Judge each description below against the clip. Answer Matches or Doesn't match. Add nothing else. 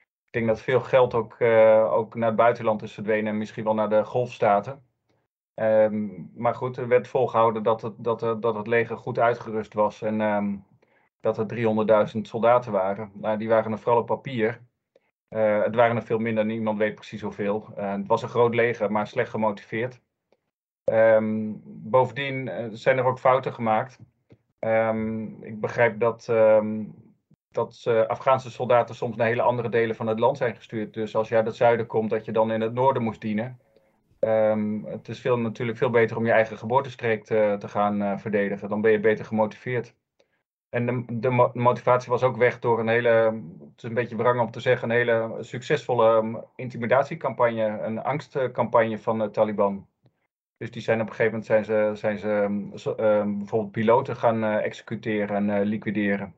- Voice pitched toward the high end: Doesn't match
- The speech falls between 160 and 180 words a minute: Doesn't match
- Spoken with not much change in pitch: Matches